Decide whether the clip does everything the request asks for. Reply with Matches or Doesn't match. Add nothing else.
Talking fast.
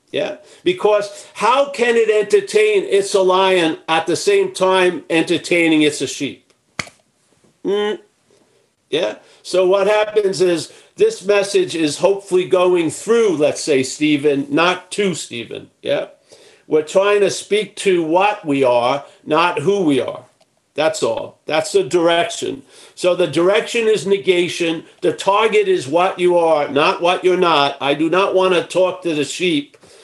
Doesn't match